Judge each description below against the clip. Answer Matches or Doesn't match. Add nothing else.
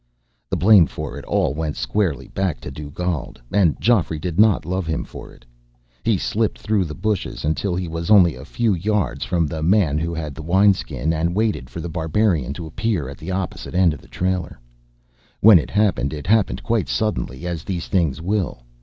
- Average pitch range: Matches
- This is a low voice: Matches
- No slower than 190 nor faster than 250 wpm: Matches